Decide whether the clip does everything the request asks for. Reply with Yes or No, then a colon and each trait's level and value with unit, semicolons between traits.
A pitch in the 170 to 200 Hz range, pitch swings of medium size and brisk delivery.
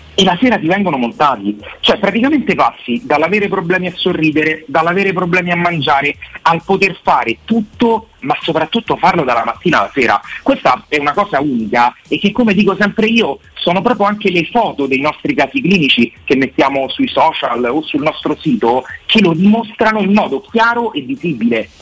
No: medium, 185 Hz; wide, 6.7 semitones; fast, 175 wpm